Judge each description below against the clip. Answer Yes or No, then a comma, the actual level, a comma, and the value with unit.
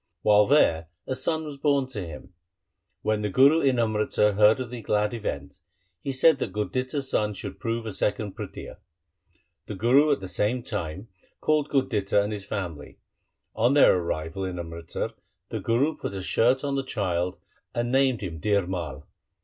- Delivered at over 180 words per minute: No, average, 175 wpm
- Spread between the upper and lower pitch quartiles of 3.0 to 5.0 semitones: No, wide, 5.6 semitones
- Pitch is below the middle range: Yes, low, 110 Hz